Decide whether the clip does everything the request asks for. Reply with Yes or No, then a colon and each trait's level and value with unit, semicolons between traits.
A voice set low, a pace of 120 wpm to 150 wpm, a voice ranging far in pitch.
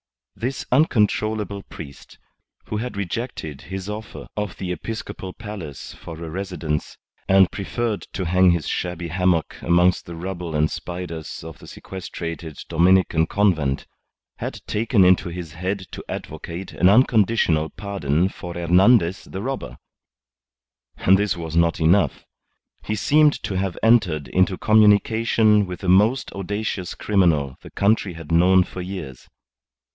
No: very low, 95 Hz; average, 140 wpm; average, 3.7 semitones